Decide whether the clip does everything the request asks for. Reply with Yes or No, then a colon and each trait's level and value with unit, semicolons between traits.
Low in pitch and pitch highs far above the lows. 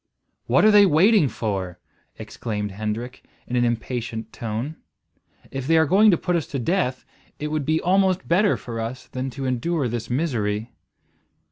Yes: low, 130 Hz; wide, 6.5 semitones